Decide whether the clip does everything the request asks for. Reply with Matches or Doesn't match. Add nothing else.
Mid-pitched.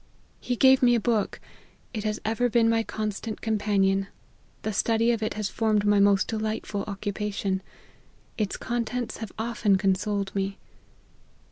Doesn't match